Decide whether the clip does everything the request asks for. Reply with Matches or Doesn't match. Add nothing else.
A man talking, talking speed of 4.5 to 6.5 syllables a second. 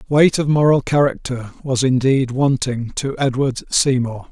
Doesn't match